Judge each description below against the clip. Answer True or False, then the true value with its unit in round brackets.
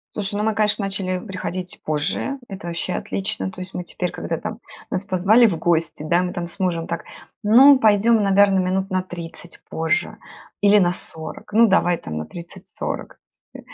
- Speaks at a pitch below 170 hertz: False (185 Hz)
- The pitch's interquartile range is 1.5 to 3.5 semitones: True (2.9 semitones)